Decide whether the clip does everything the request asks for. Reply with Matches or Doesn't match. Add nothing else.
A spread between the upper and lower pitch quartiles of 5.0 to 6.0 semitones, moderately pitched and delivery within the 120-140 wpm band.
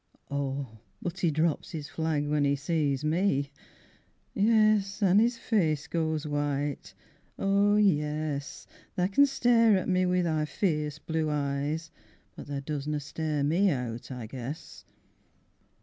Doesn't match